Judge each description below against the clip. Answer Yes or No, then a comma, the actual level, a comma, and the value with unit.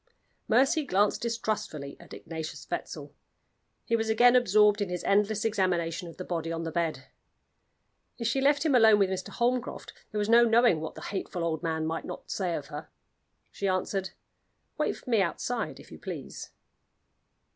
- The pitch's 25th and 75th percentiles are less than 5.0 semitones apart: No, wide, 5.6 semitones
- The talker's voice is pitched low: No, high, 200 Hz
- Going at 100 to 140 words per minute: No, average, 175 wpm